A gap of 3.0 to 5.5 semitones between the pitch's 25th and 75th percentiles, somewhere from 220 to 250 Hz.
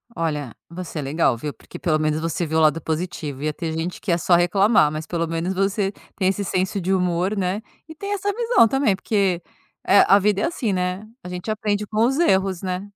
No: average, 3.7 semitones; medium, 185 Hz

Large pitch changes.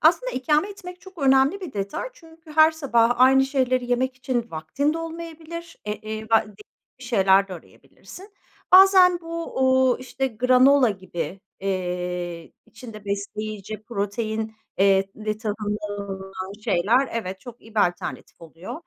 Yes: wide, 6.1 semitones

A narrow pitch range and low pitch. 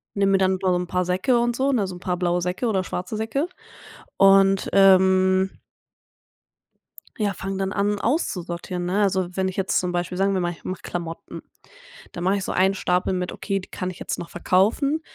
No: narrow, 1.6 semitones; high, 190 Hz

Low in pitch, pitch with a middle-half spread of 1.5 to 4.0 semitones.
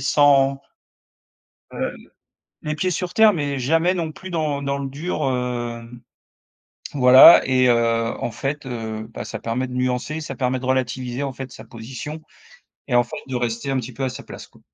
Yes: low, 130 Hz; average, 2.9 semitones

